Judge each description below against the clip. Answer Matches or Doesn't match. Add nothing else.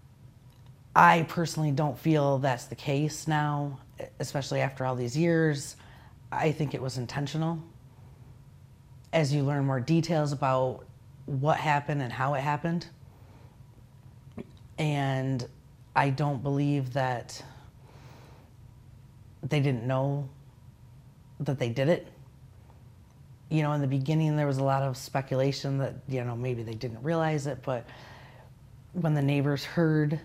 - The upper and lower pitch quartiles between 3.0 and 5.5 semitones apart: Doesn't match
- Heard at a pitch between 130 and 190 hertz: Matches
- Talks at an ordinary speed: Doesn't match